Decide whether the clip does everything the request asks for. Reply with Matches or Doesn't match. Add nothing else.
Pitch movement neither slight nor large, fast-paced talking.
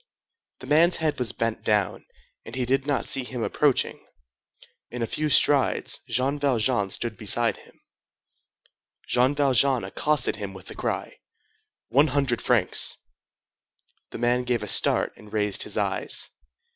Doesn't match